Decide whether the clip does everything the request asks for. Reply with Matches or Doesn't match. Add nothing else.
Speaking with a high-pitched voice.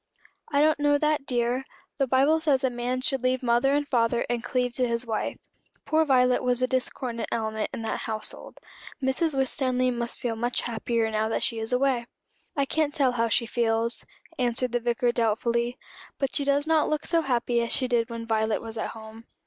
Matches